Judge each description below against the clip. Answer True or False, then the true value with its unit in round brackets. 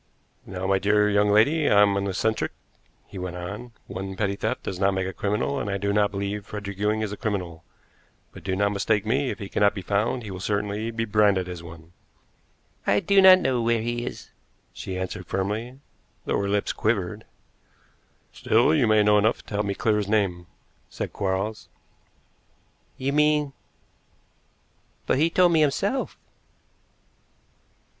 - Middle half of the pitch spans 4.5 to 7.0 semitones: False (2.8 semitones)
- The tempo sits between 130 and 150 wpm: False (175 wpm)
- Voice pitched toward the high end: False (105 Hz)